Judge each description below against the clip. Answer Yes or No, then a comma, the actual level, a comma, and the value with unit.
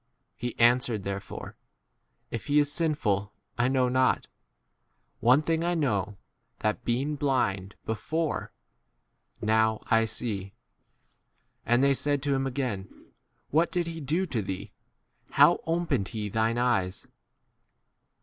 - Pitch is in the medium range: No, low, 125 Hz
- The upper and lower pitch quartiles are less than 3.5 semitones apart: No, wide, 5.4 semitones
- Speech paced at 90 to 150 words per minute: Yes, average, 140 wpm